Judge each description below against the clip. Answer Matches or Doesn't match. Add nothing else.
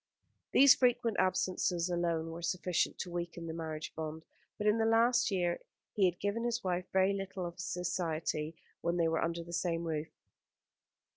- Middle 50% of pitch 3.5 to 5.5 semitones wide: Doesn't match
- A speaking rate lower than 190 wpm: Matches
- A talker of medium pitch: Matches